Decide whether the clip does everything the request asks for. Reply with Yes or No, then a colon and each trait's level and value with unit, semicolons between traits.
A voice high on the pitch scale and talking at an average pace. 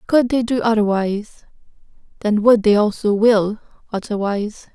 No: high, 215 Hz; slow, 125 wpm